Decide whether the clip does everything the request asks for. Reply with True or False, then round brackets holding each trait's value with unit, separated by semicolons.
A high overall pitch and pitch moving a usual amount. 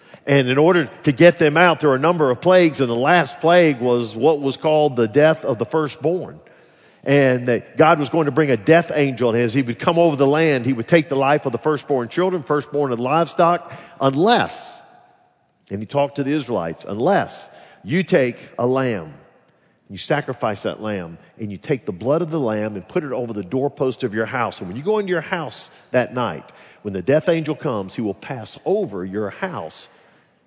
False (140 Hz; 5.0 semitones)